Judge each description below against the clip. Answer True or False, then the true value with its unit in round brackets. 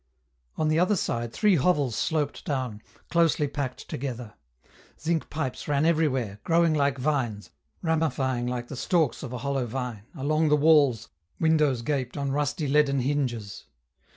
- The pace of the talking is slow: False (150 wpm)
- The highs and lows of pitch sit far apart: False (3.7 semitones)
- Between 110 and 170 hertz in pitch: True (140 Hz)